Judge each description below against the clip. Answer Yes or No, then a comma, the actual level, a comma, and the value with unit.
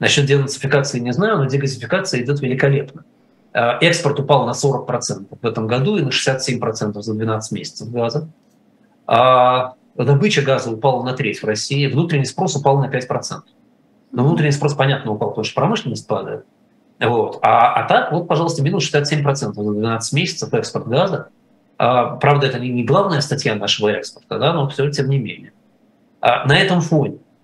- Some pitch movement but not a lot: Yes, average, 3.1 semitones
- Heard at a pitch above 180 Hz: No, low, 135 Hz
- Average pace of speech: No, fast, 165 wpm